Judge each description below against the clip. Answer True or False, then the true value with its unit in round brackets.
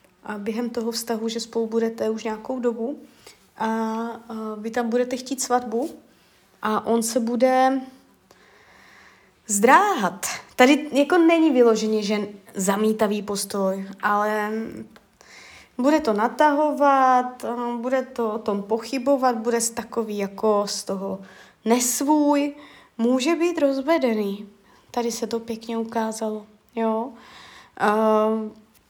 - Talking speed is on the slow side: True (110 wpm)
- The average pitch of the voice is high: True (230 Hz)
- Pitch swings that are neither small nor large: True (3.0 semitones)